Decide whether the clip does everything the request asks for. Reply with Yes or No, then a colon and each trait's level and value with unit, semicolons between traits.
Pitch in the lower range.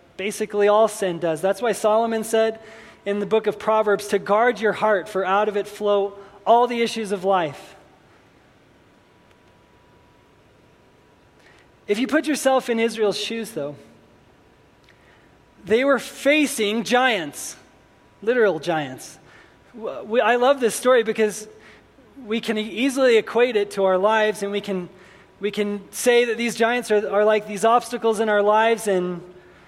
No: high, 215 Hz